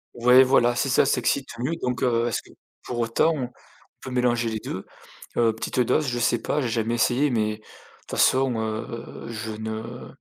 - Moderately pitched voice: No, low, 120 Hz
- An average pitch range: No, narrow, 2.0 semitones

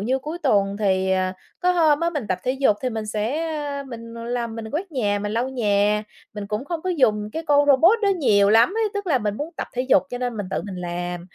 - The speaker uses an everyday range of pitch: No, wide, 5.8 semitones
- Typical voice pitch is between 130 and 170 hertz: No, high, 235 Hz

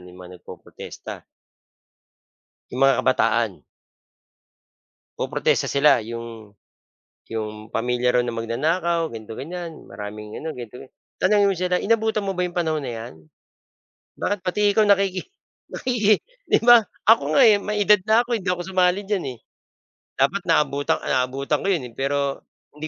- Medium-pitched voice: Yes, medium, 150 Hz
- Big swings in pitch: Yes, wide, 8.7 semitones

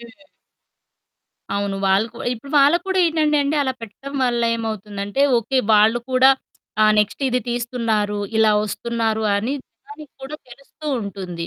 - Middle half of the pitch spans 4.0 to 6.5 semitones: Yes, average, 4.8 semitones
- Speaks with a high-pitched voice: Yes, high, 235 Hz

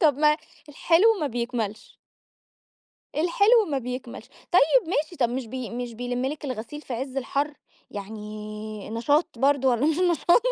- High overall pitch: Yes, very high, 265 Hz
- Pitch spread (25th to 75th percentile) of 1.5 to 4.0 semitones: No, average, 4.6 semitones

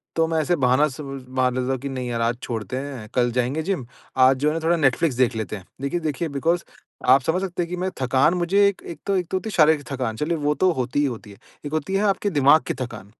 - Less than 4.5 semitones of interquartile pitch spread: No, average, 4.9 semitones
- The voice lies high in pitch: No, medium, 145 Hz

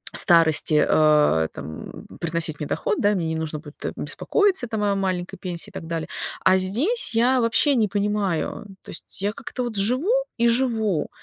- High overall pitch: Yes, high, 195 Hz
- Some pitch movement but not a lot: No, wide, 6.0 semitones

